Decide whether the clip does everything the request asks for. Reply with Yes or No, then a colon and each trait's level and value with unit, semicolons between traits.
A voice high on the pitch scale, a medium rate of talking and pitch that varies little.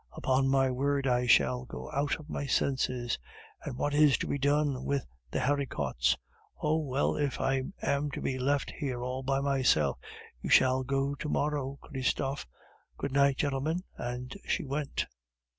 No: low, 135 Hz; average, 165 wpm; narrow, 1.8 semitones